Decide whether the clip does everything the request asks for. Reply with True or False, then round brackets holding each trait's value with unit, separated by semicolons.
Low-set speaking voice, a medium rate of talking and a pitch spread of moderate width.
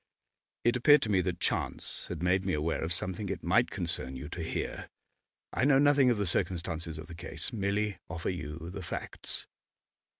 True (90 Hz; 190 wpm; 4.2 semitones)